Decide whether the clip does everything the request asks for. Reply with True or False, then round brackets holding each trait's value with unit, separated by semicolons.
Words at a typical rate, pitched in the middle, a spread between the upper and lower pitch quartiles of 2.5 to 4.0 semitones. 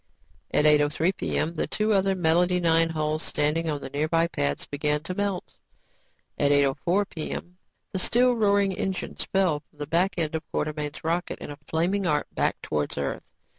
True (170 wpm; 165 Hz; 3.7 semitones)